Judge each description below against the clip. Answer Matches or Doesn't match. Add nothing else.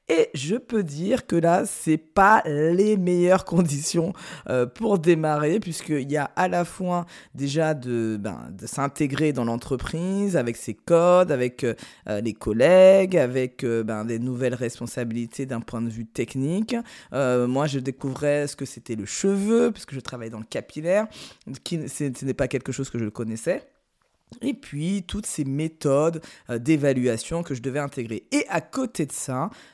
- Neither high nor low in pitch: Matches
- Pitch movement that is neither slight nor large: Doesn't match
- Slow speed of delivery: Doesn't match